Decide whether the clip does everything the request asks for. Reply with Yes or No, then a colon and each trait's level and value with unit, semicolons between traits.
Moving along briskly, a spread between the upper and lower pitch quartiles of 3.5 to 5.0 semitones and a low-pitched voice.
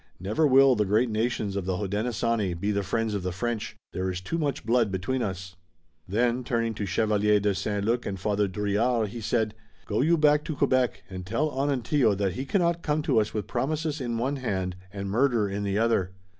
Yes: fast, 210 wpm; average, 4.2 semitones; low, 110 Hz